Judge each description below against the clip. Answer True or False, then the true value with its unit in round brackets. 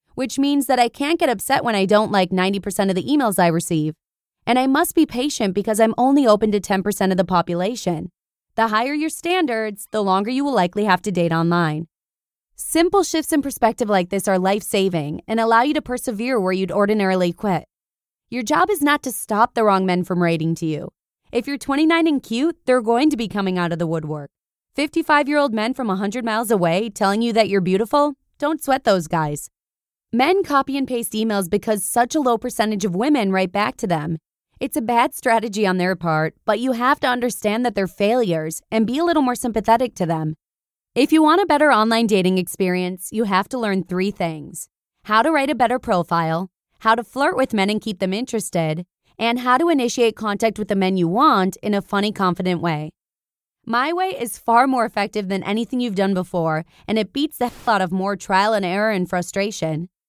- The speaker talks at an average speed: False (215 wpm)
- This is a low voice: False (215 Hz)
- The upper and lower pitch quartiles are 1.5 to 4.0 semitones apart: False (5.2 semitones)